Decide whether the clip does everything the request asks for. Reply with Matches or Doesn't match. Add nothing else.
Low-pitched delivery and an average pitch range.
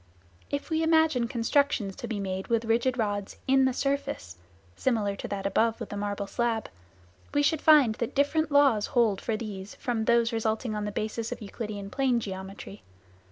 Doesn't match